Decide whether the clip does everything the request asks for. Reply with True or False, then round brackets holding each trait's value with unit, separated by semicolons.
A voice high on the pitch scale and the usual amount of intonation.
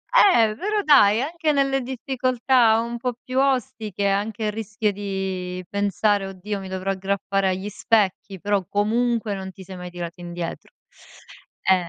True (205 Hz; 4.0 semitones)